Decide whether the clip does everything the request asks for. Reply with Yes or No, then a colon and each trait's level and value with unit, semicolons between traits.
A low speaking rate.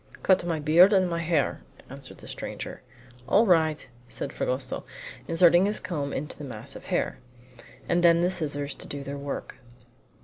No: average, 170 wpm